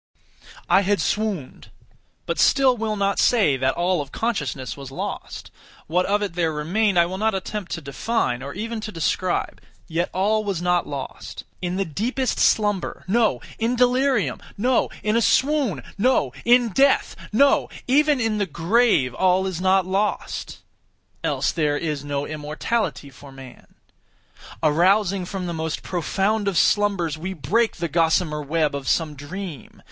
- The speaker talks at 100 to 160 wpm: Yes, average, 150 wpm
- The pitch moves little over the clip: No, wide, 5.6 semitones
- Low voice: No, medium, 185 Hz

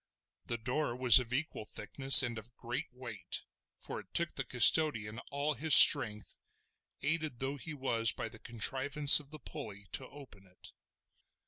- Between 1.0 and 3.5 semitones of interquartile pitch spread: No, average, 4.2 semitones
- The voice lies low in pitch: Yes, low, 130 Hz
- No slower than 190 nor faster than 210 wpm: No, average, 160 wpm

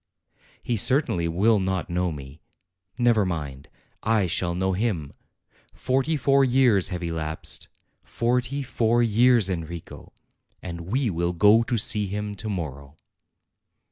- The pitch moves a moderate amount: No, wide, 5.7 semitones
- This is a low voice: Yes, low, 100 Hz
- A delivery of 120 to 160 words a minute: Yes, slow, 135 wpm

